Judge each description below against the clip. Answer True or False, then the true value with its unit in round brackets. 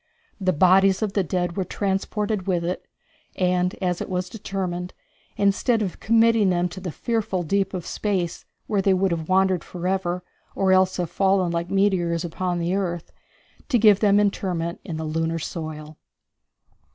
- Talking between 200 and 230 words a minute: False (165 wpm)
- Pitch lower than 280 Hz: True (185 Hz)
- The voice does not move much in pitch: True (2.1 semitones)